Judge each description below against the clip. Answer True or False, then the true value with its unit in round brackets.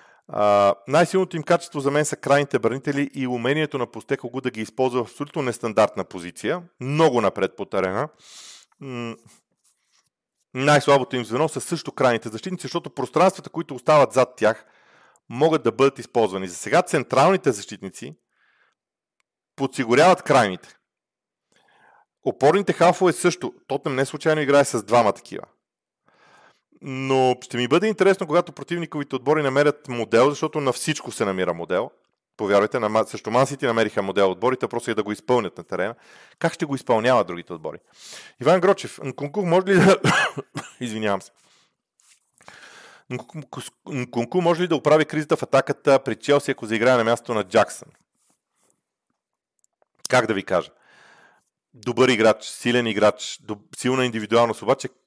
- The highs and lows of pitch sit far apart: False (4.6 semitones)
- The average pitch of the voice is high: False (135 Hz)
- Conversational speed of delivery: True (140 wpm)